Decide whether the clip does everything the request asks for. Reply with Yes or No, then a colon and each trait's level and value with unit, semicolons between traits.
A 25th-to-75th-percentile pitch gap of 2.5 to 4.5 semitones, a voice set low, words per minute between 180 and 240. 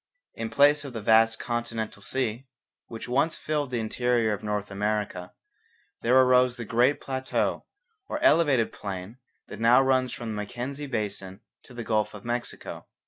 No: average, 3.3 semitones; low, 120 Hz; average, 160 wpm